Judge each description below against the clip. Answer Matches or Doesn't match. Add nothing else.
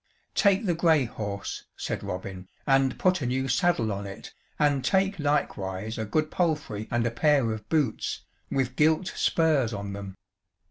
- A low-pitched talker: Matches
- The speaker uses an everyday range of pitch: Doesn't match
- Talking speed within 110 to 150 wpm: Doesn't match